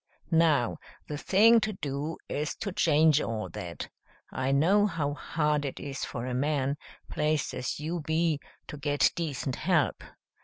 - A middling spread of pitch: Yes, average, 3.1 semitones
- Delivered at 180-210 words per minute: No, average, 155 wpm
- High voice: No, medium, 150 Hz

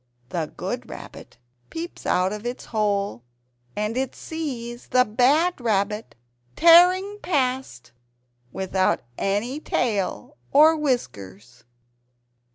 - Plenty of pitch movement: Yes, wide, 7.0 semitones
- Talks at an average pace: No, slow, 100 wpm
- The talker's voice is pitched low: No, high, 240 Hz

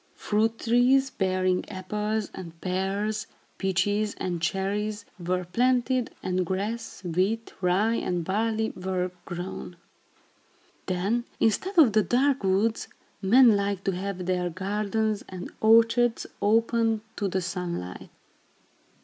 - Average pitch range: Yes, average, 3.5 semitones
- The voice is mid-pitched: No, high, 200 Hz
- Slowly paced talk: Yes, slow, 115 wpm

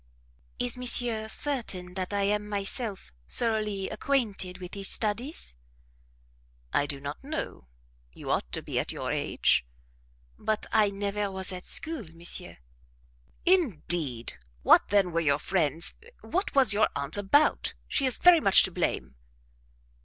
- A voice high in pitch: Yes, high, 200 Hz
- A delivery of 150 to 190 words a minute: No, average, 140 wpm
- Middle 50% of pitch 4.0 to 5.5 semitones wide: Yes, average, 5.1 semitones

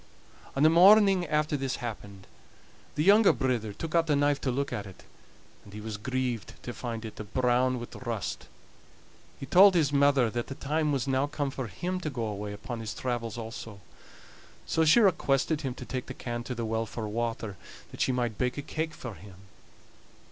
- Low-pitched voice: Yes, low, 130 Hz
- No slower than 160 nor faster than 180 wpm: No, average, 200 wpm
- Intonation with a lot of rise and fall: No, average, 4.5 semitones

